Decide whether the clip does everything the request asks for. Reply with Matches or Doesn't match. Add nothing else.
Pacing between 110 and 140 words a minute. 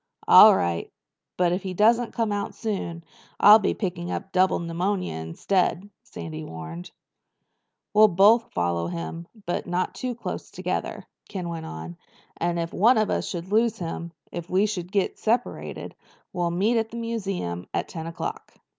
Doesn't match